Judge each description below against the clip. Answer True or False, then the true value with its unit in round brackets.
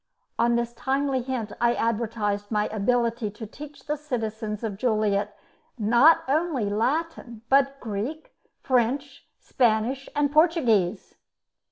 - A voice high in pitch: True (235 Hz)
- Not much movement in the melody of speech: False (4.2 semitones)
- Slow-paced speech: True (120 wpm)